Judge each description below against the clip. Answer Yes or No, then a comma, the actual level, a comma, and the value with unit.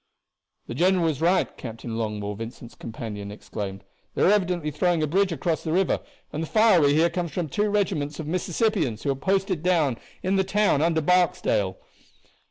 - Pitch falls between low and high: Yes, medium, 165 Hz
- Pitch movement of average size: No, wide, 6.1 semitones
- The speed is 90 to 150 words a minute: No, average, 180 wpm